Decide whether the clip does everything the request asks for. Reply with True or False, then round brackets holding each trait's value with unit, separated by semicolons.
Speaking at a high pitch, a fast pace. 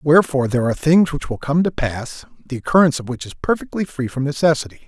False (140 Hz; 220 wpm)